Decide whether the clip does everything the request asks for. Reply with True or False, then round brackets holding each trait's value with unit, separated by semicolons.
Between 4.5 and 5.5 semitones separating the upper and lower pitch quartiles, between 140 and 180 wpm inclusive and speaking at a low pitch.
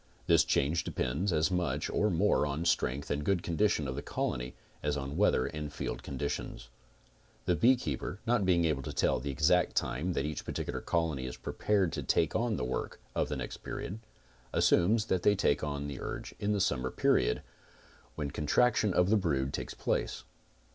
False (5.2 semitones; 190 wpm; 80 Hz)